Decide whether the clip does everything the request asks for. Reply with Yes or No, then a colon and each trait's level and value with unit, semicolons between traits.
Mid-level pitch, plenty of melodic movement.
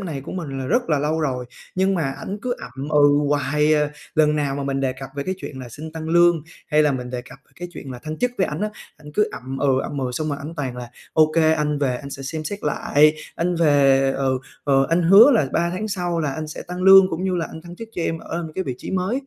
No: medium, 150 Hz; average, 4.0 semitones